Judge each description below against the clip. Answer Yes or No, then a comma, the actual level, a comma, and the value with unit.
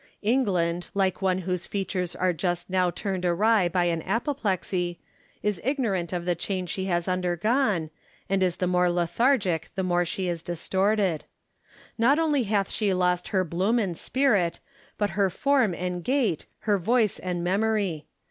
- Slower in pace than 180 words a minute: Yes, average, 160 wpm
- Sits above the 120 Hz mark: Yes, medium, 185 Hz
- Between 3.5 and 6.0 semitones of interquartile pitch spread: No, average, 3.1 semitones